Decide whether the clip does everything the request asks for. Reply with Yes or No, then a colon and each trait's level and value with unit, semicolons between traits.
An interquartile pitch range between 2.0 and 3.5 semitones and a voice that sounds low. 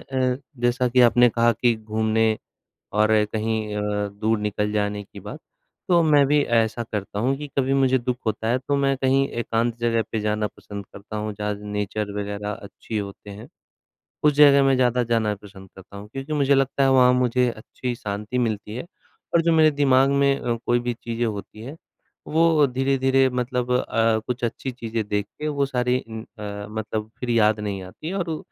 No: average, 3.9 semitones; low, 120 Hz